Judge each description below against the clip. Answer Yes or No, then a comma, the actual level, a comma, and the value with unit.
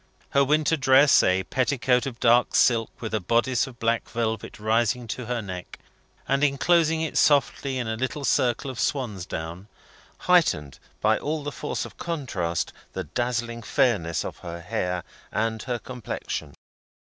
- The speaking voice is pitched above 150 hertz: No, low, 120 Hz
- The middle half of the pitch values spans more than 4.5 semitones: No, average, 4.1 semitones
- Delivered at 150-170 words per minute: Yes, average, 155 wpm